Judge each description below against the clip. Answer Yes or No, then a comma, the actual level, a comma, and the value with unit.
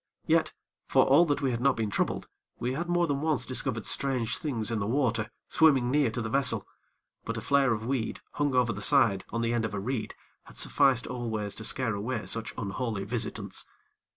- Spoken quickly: Yes, fast, 210 wpm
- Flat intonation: No, average, 3.5 semitones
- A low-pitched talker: Yes, low, 120 Hz